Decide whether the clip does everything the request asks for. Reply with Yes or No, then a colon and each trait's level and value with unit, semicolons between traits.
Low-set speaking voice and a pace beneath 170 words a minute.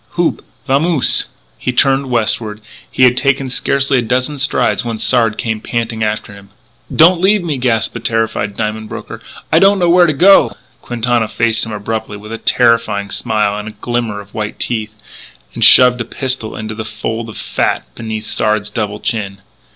No: low, 115 Hz; average, 180 wpm